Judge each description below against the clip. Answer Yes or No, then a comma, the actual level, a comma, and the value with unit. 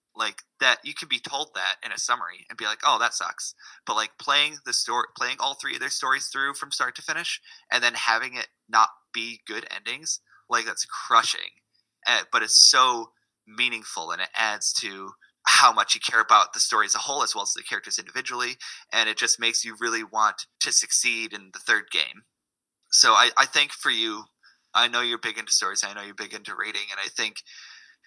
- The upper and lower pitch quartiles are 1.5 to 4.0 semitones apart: Yes, average, 3.4 semitones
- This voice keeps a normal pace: No, fast, 215 wpm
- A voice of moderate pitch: No, low, 115 Hz